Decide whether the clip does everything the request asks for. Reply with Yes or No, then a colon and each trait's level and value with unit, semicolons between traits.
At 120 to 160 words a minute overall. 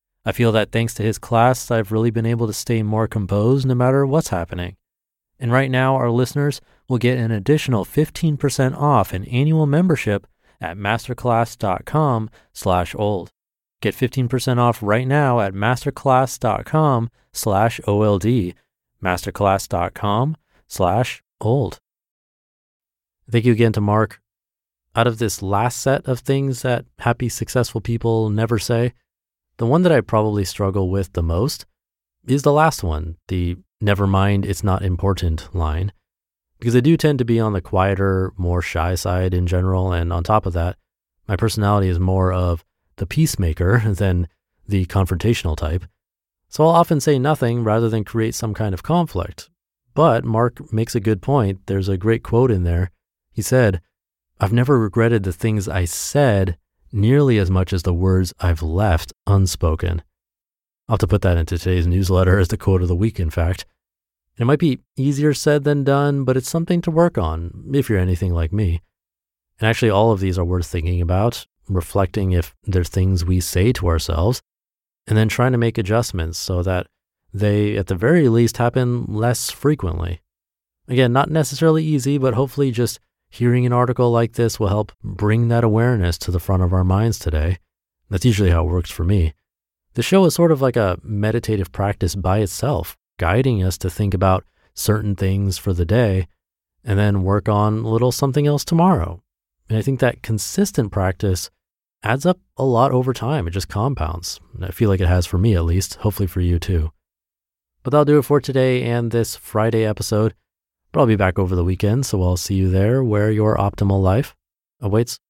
No: average, 180 wpm